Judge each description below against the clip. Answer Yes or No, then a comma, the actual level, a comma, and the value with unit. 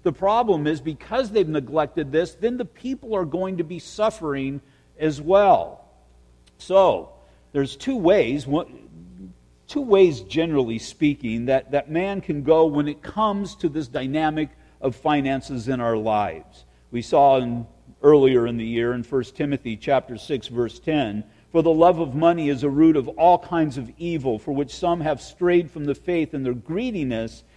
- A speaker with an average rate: Yes, average, 170 wpm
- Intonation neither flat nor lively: No, wide, 5.8 semitones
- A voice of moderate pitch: Yes, medium, 150 Hz